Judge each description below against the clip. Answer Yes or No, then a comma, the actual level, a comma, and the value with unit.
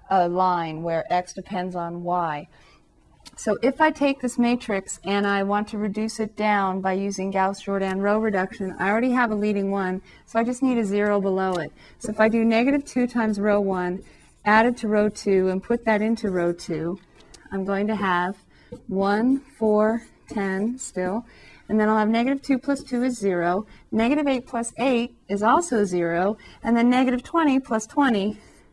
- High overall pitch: Yes, high, 210 Hz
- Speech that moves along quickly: No, average, 190 wpm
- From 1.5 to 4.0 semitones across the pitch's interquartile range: Yes, average, 3.7 semitones